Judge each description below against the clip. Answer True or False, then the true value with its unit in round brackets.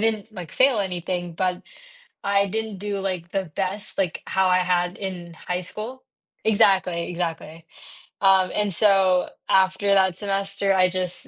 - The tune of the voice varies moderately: False (1.8 semitones)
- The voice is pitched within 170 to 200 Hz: True (190 Hz)